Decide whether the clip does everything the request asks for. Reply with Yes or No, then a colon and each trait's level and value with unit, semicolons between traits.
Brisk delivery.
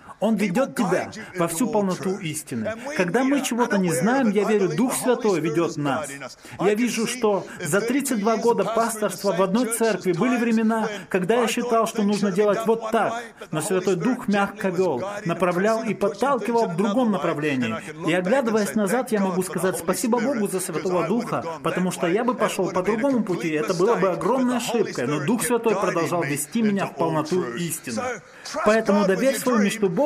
Yes: fast, 175 wpm